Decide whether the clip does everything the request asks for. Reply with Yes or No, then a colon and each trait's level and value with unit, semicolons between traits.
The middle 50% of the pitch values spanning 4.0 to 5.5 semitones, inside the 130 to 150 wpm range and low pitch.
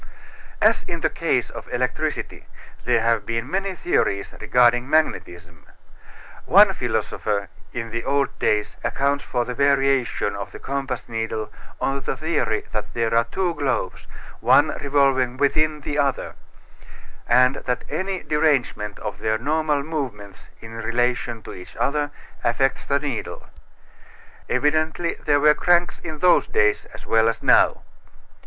Yes: average, 4.5 semitones; average, 140 wpm; low, 130 Hz